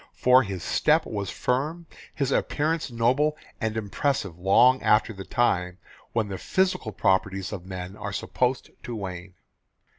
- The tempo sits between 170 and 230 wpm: No, average, 145 wpm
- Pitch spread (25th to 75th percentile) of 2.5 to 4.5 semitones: No, average, 5.3 semitones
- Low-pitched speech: Yes, low, 110 Hz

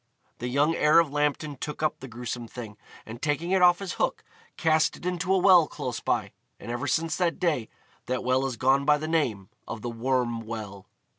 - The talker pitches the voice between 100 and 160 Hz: Yes, medium, 140 Hz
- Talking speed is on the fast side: Yes, fast, 210 wpm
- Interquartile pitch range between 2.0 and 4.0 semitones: No, average, 5.2 semitones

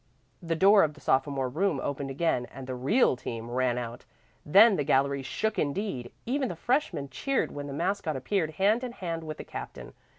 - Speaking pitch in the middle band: Yes, medium, 155 Hz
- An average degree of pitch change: No, wide, 6.9 semitones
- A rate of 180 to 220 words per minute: Yes, average, 195 wpm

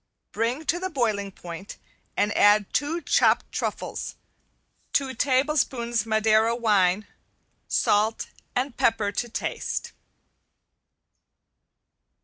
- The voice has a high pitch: Yes, high, 225 Hz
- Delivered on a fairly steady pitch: No, average, 4.0 semitones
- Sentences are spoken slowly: Yes, slow, 95 wpm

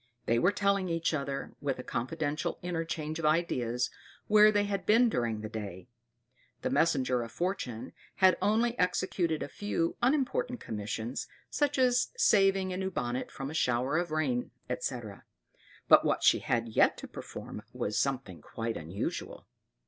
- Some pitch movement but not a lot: No, wide, 8.2 semitones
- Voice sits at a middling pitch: Yes, medium, 155 Hz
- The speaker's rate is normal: Yes, average, 155 wpm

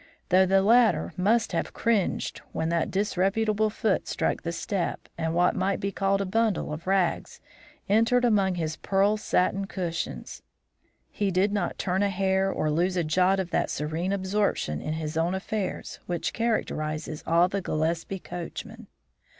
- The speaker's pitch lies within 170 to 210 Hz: Yes, high, 190 Hz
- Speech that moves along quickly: No, average, 160 wpm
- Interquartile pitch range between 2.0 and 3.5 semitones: Yes, average, 2.9 semitones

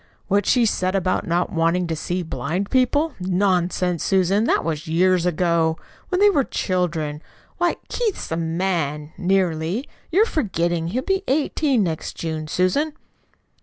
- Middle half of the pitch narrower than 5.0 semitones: No, wide, 5.4 semitones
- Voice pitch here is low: No, medium, 180 Hz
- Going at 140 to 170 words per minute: Yes, average, 145 wpm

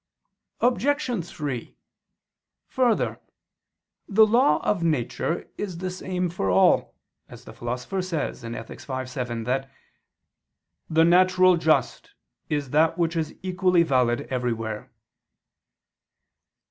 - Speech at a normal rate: No, slow, 110 wpm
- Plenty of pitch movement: Yes, wide, 6.4 semitones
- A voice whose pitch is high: No, medium, 165 Hz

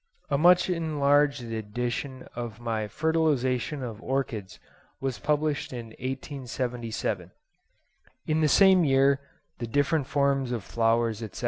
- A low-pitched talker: Yes, low, 130 Hz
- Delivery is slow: Yes, slow, 120 wpm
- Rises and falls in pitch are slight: No, average, 3.8 semitones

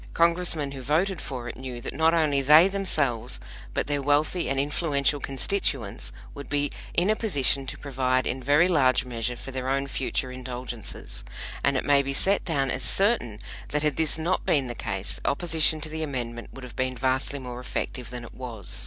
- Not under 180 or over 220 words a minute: Yes, average, 195 wpm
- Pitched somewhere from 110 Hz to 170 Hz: Yes, medium, 140 Hz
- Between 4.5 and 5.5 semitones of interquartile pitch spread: No, average, 3.5 semitones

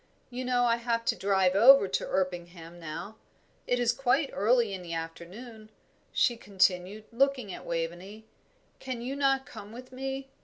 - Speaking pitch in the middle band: No, high, 220 Hz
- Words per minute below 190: Yes, average, 160 wpm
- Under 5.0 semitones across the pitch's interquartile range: No, average, 5.3 semitones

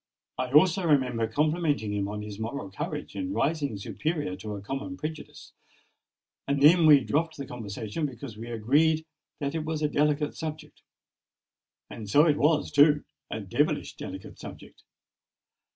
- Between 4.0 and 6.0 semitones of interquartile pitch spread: Yes, wide, 5.4 semitones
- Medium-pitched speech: Yes, medium, 145 Hz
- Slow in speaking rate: No, average, 150 wpm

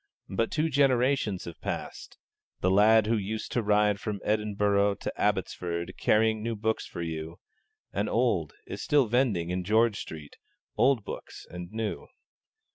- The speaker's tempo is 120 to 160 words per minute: Yes, average, 150 wpm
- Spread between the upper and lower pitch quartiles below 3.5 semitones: Yes, average, 3.1 semitones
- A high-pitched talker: No, low, 105 Hz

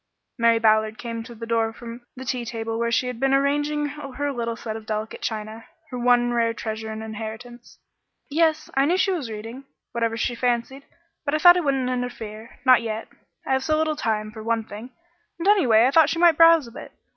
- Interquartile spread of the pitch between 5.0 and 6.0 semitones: No, average, 3.7 semitones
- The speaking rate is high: Yes, fast, 215 wpm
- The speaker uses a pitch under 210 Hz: No, high, 240 Hz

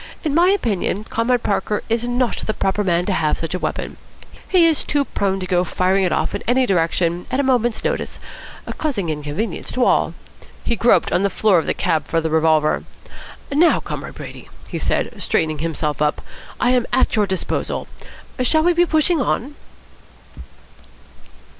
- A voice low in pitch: No, high, 210 Hz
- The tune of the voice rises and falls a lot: Yes, wide, 7.0 semitones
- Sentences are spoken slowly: No, average, 180 wpm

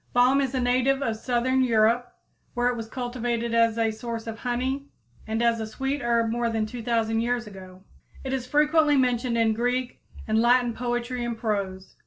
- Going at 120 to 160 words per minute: No, average, 185 wpm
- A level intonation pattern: Yes, narrow, 1.9 semitones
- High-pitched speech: Yes, high, 240 Hz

